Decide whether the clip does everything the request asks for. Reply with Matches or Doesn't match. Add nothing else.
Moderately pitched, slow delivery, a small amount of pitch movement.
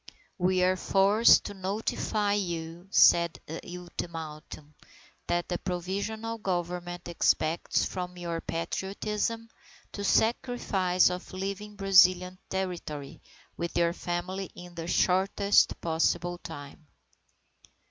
Matches